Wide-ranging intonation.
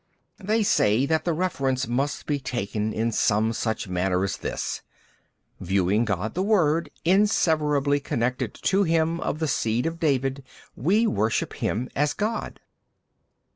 Yes: wide, 6.8 semitones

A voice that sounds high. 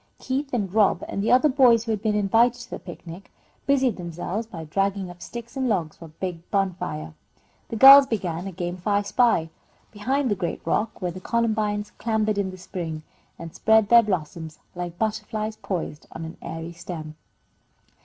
Yes: high, 200 Hz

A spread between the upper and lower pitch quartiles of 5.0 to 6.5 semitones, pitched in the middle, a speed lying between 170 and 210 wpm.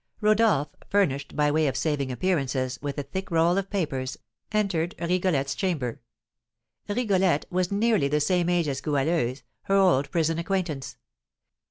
No: average, 5.3 semitones; medium, 165 Hz; average, 145 wpm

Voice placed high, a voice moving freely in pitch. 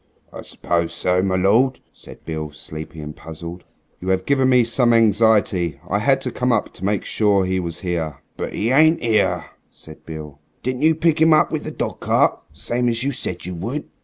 No: low, 100 Hz; wide, 6.6 semitones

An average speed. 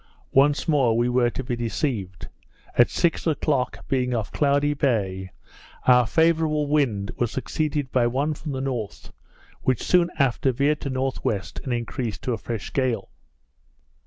Yes: average, 155 wpm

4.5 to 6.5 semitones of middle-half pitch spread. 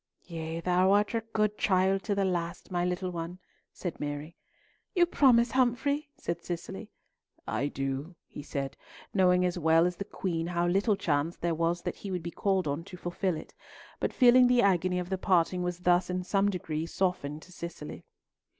No: average, 2.7 semitones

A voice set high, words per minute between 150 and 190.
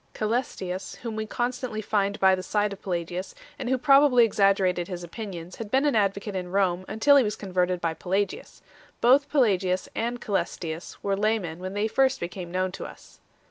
Yes: high, 200 Hz; average, 180 wpm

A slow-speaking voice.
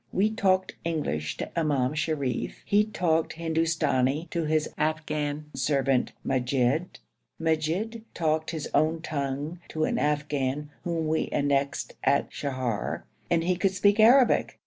Yes: slow, 130 wpm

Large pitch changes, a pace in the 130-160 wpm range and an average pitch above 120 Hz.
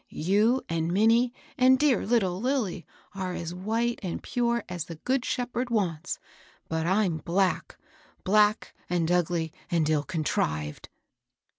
Yes: wide, 5.8 semitones; average, 140 wpm; high, 190 Hz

